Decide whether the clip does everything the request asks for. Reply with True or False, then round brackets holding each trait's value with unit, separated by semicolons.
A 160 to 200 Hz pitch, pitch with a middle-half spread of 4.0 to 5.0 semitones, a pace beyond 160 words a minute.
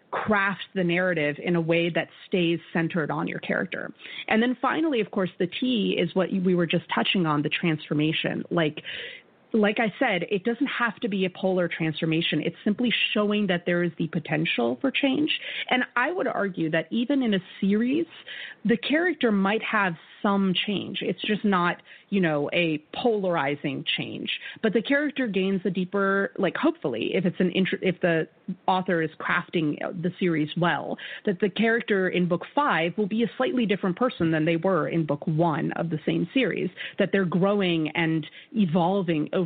True (185 Hz; 4.3 semitones; 185 wpm)